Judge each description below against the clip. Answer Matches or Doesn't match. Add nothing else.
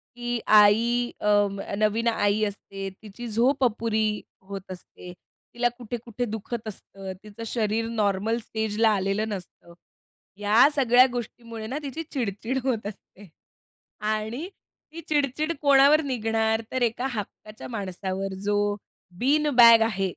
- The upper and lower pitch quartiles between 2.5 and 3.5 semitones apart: Matches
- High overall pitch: Matches